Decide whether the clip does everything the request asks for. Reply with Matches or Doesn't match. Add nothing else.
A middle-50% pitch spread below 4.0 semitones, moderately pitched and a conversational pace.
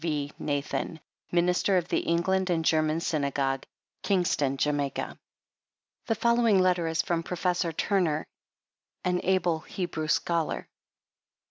Doesn't match